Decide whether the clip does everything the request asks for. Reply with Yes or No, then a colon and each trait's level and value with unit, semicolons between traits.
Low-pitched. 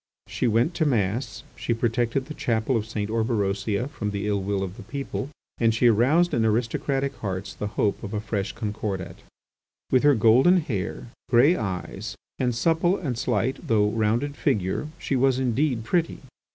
Yes: low, 115 Hz